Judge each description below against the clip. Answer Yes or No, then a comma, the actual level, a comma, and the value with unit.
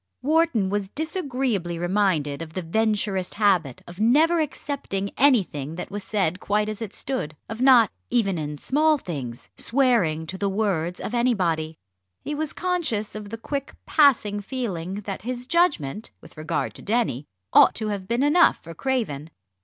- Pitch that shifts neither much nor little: No, wide, 6.7 semitones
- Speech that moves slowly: No, average, 160 wpm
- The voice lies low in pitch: No, high, 210 Hz